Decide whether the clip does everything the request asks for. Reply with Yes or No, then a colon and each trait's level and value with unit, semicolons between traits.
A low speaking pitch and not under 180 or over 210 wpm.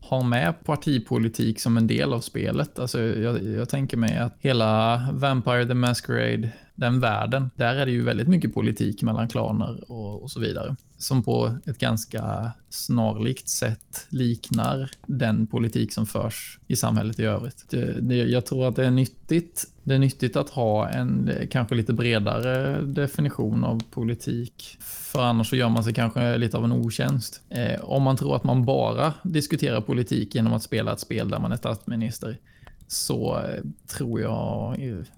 No: low, 120 Hz; average, 170 wpm